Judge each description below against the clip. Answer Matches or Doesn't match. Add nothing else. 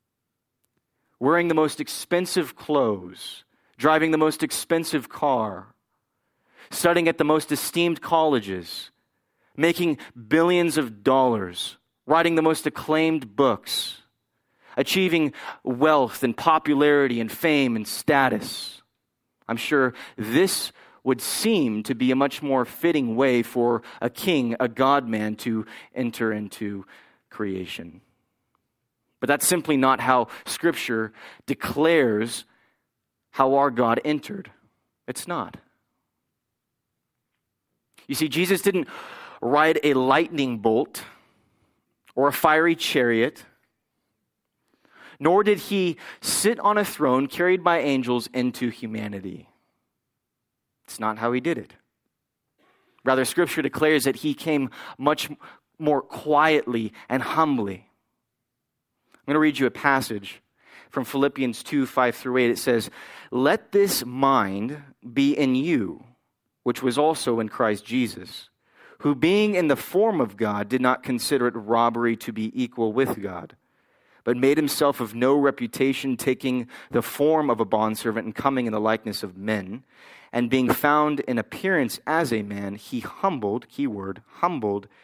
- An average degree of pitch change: Matches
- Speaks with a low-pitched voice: Matches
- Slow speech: Matches